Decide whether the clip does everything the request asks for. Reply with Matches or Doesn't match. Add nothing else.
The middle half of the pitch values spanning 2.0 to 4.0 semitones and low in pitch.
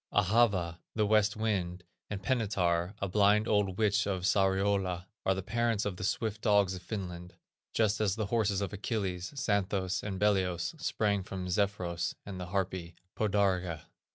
Matches